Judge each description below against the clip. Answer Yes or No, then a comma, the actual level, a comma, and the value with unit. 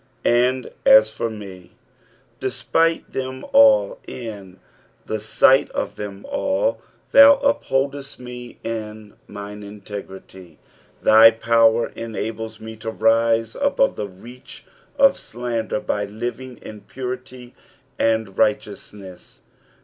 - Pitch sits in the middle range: No, low, 115 Hz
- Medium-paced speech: No, slow, 120 wpm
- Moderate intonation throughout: Yes, average, 3.5 semitones